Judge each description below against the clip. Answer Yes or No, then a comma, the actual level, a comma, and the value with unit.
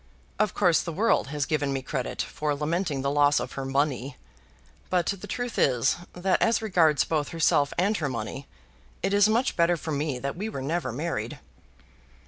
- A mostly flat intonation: No, average, 4.8 semitones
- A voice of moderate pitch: Yes, medium, 155 Hz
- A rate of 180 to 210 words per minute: Yes, average, 185 wpm